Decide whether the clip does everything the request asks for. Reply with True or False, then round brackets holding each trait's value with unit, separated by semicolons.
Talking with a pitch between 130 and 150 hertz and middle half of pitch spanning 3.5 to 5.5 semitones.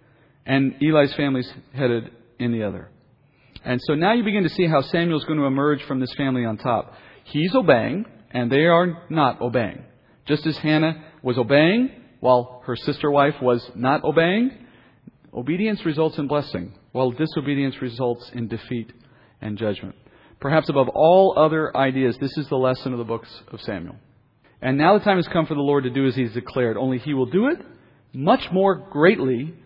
True (135 Hz; 4.1 semitones)